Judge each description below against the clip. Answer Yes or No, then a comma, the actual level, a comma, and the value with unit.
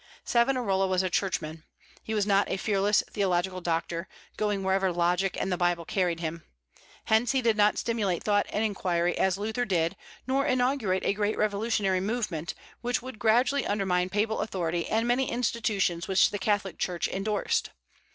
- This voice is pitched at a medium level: No, high, 200 Hz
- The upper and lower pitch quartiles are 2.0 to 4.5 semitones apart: Yes, average, 3.4 semitones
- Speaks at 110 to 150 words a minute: No, average, 165 wpm